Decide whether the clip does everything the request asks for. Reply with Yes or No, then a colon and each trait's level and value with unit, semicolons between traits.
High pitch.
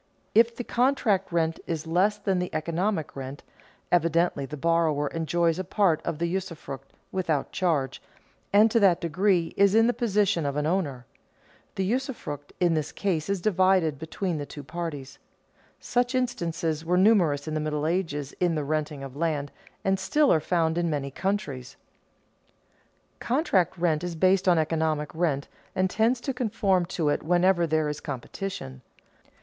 No: medium, 170 Hz